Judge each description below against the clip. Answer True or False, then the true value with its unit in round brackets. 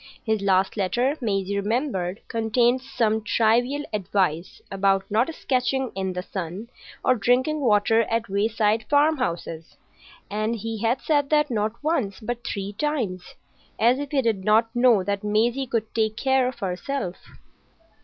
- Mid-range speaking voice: False (225 Hz)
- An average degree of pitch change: True (4.1 semitones)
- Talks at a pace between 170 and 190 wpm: False (145 wpm)